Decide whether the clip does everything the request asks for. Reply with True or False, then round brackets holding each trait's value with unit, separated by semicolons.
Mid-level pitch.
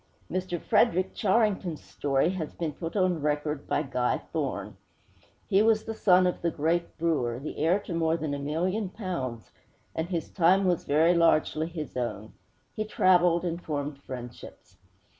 True (170 Hz)